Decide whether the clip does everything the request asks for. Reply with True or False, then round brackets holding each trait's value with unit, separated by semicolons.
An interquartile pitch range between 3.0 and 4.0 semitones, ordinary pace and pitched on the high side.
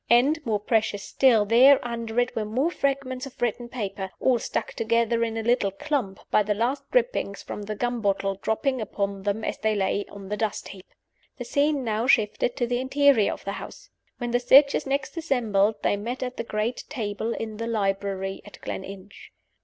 True (3.7 semitones; 195 wpm; 230 Hz)